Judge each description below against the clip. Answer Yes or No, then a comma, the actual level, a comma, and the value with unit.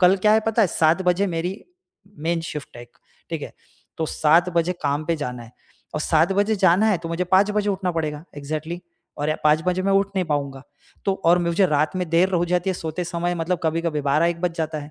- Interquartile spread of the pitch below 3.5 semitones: Yes, average, 2.8 semitones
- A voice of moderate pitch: Yes, medium, 170 Hz